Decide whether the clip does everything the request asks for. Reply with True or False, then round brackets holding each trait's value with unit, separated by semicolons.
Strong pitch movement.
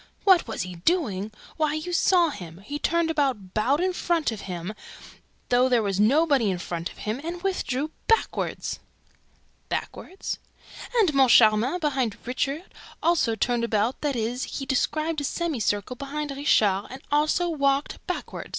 True (6.3 semitones)